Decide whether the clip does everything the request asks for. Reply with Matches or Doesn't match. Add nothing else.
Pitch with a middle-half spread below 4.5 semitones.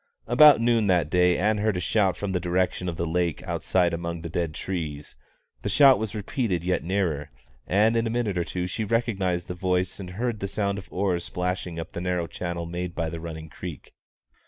Matches